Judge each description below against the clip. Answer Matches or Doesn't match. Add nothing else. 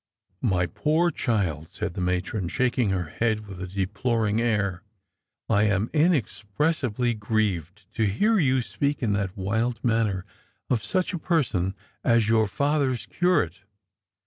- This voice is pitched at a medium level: Doesn't match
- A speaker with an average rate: Matches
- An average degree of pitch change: Matches